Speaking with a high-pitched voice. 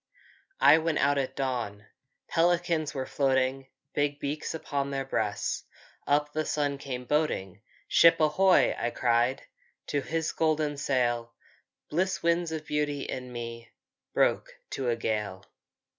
No: medium, 140 Hz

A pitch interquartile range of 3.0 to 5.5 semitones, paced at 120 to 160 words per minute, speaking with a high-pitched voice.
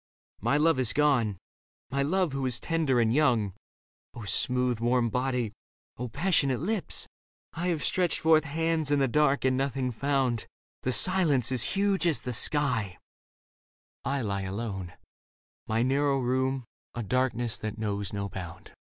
No: average, 4.2 semitones; average, 155 wpm; low, 130 Hz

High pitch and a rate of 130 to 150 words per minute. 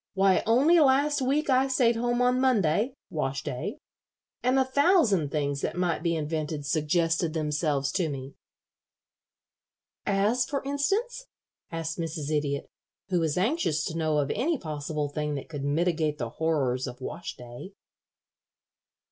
No: medium, 165 Hz; average, 145 wpm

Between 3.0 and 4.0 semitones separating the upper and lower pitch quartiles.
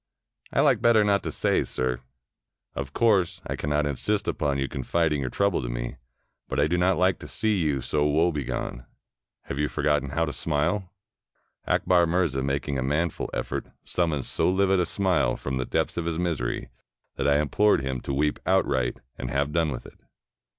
No: average, 4.6 semitones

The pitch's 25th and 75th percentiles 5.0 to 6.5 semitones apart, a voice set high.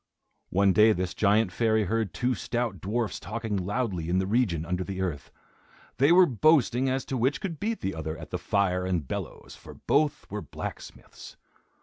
No: average, 5.3 semitones; low, 105 Hz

